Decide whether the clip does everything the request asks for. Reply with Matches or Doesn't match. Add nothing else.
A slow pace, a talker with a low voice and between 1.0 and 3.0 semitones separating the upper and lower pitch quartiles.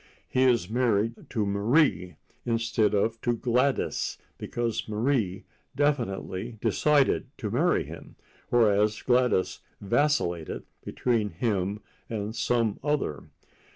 Doesn't match